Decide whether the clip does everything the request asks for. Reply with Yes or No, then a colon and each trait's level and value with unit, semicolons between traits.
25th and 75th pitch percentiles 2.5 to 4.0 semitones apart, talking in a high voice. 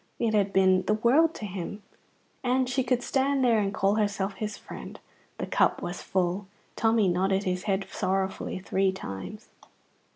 Yes: average, 3.3 semitones; high, 200 Hz